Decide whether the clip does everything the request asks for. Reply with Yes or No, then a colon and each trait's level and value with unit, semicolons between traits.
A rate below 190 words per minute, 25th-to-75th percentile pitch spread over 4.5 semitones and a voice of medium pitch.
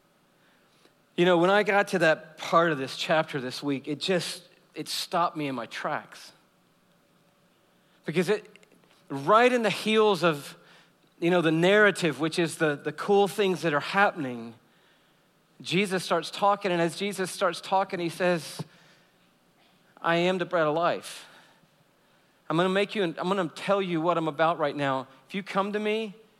No: average, 175 wpm; average, 3.7 semitones; medium, 180 Hz